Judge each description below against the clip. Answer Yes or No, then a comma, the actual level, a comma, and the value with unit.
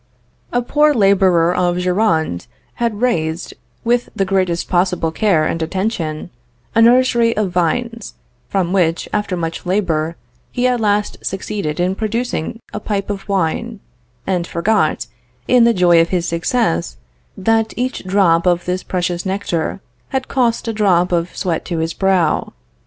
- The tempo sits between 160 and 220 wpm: No, average, 150 wpm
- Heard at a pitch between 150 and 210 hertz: Yes, high, 190 Hz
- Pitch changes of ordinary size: Yes, average, 4.5 semitones